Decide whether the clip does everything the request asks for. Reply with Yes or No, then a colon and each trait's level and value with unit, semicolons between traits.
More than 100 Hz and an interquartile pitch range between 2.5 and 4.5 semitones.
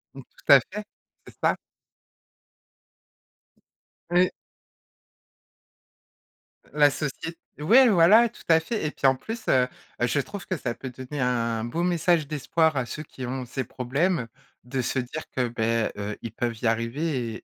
No: low, 135 Hz; wide, 5.4 semitones